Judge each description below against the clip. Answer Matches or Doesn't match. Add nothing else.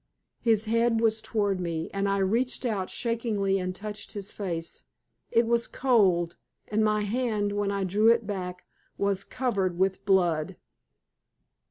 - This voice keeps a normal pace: Matches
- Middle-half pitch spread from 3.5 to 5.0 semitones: Doesn't match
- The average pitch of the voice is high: Matches